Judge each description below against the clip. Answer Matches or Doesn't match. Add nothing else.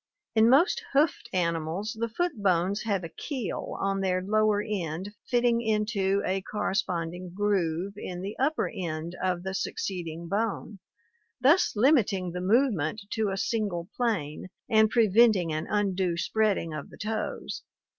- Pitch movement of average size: Matches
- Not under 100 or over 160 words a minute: Matches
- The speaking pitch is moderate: Doesn't match